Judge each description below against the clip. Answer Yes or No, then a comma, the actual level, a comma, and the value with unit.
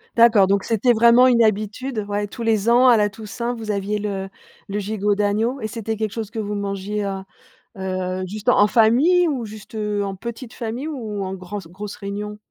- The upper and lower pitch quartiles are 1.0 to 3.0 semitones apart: Yes, narrow, 2.6 semitones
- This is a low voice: No, high, 210 Hz